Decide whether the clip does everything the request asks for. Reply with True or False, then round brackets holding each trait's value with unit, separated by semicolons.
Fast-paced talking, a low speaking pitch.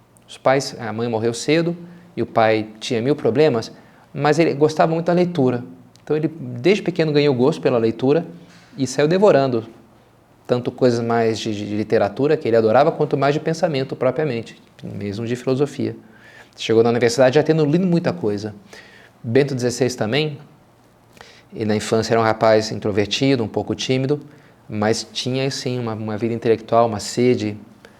False (165 wpm; 125 Hz)